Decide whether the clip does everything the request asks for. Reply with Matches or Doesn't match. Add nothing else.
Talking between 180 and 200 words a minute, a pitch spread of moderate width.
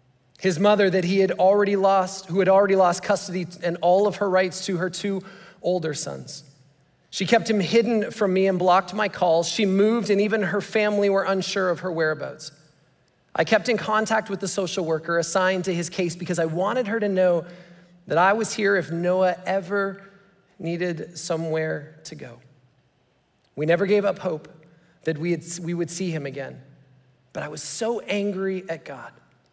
Matches